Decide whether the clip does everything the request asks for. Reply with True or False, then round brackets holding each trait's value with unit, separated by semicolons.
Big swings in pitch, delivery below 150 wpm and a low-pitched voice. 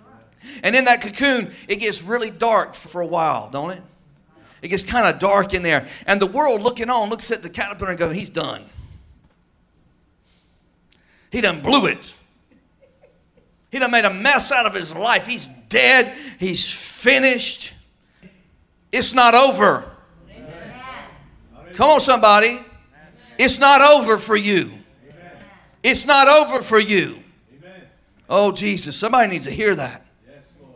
False (6.2 semitones; 140 wpm; 210 Hz)